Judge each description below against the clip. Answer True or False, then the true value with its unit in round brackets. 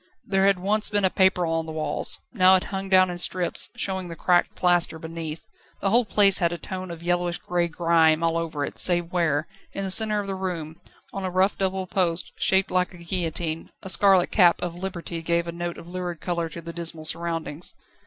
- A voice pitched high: False (175 Hz)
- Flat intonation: True (2.1 semitones)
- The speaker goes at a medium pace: False (215 wpm)